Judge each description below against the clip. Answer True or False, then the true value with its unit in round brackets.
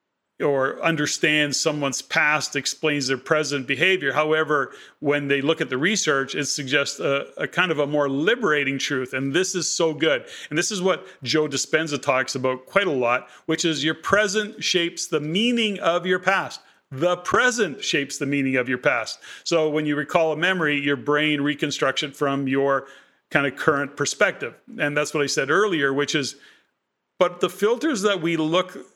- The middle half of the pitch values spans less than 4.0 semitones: True (3.2 semitones)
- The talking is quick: False (185 wpm)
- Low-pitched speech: False (150 Hz)